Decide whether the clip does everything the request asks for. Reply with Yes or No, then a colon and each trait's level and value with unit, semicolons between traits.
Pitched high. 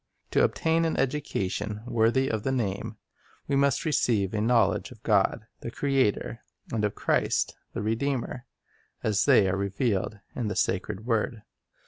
No: low, 115 Hz